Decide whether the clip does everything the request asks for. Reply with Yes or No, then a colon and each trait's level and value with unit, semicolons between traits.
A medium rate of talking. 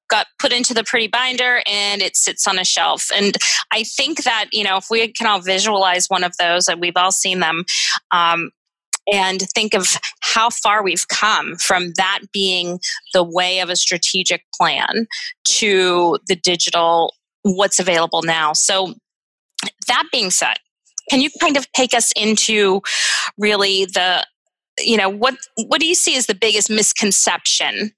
Yes: average, 165 wpm